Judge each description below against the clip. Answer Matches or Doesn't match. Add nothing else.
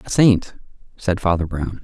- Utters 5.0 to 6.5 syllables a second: Doesn't match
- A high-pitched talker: Doesn't match